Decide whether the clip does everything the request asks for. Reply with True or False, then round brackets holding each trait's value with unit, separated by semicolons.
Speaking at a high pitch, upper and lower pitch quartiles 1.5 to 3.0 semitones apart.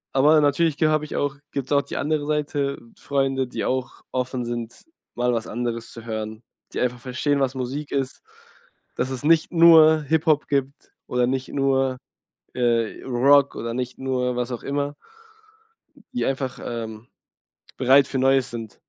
False (135 Hz; 2.7 semitones)